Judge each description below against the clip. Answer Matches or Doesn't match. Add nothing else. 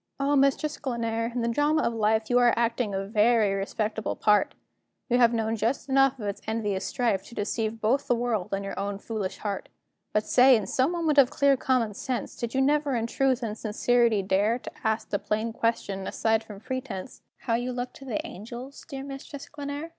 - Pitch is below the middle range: Doesn't match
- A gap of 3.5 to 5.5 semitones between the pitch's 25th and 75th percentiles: Matches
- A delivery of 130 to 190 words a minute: Doesn't match